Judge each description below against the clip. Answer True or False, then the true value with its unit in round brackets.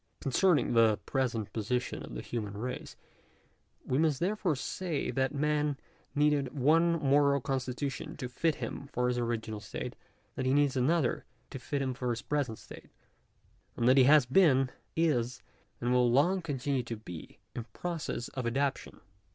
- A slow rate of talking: False (160 wpm)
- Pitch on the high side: False (135 Hz)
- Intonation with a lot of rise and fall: False (3.3 semitones)